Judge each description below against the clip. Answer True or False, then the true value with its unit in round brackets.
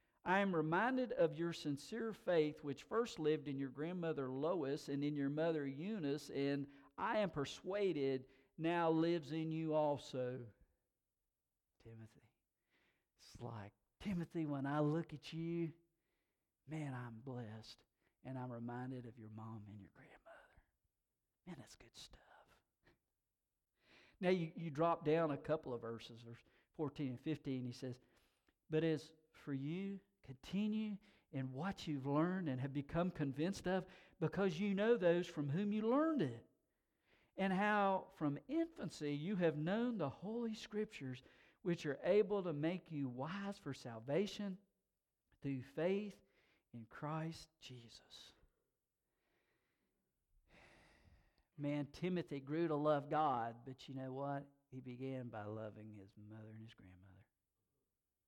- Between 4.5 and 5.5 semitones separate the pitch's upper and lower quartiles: True (5.1 semitones)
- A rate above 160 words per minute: False (140 wpm)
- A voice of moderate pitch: True (150 Hz)